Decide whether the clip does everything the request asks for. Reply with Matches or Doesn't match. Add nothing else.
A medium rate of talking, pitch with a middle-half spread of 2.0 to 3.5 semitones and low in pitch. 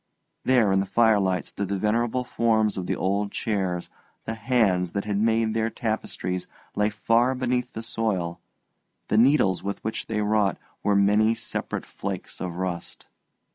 Matches